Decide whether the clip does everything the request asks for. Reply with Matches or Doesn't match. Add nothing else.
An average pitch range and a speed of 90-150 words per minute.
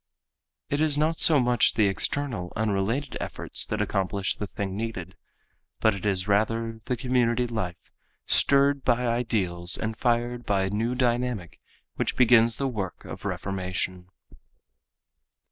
Matches